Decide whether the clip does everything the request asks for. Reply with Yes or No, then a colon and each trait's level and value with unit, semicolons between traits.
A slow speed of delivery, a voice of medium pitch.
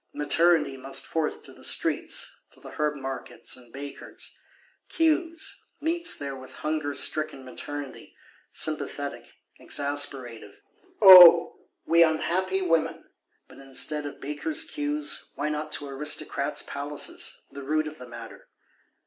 Yes: slow, 125 wpm; medium, 150 Hz